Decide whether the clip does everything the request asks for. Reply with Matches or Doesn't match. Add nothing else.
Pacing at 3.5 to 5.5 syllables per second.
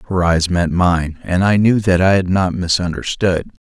Matches